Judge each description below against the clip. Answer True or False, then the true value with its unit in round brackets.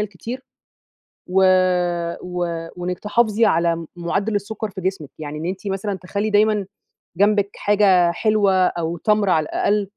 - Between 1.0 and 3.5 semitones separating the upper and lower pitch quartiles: True (3.1 semitones)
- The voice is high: True (195 Hz)